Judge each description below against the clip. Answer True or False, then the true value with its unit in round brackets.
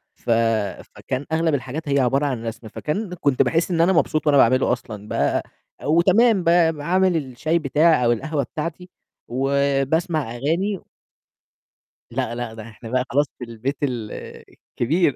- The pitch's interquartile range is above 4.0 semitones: True (4.9 semitones)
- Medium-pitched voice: True (145 Hz)